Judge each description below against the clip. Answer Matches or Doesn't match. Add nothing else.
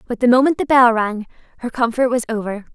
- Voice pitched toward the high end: Matches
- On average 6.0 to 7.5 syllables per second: Matches